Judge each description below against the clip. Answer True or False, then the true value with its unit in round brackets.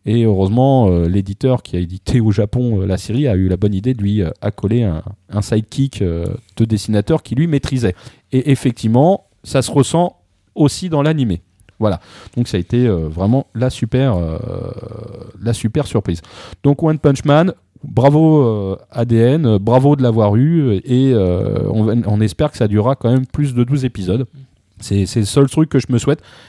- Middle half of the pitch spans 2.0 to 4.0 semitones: False (4.8 semitones)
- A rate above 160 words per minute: True (175 wpm)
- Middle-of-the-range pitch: False (120 Hz)